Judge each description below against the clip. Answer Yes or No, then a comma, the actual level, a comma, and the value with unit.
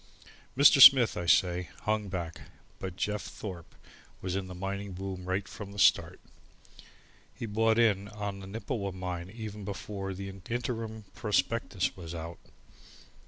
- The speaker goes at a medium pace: Yes, average, 145 wpm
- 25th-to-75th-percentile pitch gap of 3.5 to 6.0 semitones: No, narrow, 2.6 semitones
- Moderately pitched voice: No, low, 100 Hz